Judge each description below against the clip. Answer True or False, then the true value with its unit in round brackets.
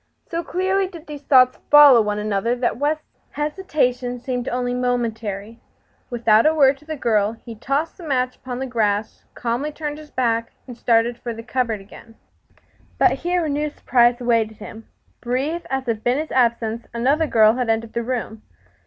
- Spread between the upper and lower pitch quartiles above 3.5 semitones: True (4.2 semitones)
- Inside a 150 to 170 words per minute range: False (180 wpm)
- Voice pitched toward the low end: False (245 Hz)